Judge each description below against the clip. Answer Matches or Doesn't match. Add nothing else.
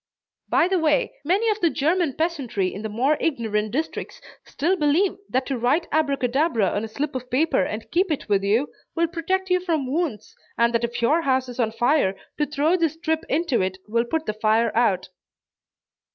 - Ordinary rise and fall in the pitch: Doesn't match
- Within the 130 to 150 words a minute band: Doesn't match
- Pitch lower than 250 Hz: Doesn't match